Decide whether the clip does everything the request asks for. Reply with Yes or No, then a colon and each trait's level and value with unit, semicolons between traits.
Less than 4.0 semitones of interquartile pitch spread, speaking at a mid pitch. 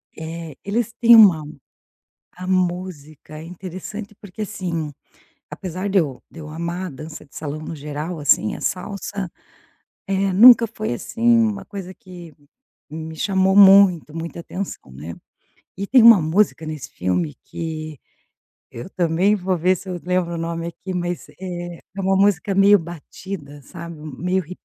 Yes: average, 3.5 semitones; medium, 180 Hz